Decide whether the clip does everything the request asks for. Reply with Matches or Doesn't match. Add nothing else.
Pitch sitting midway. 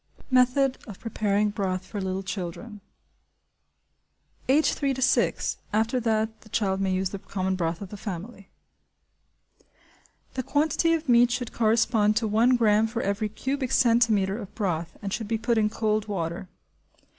Doesn't match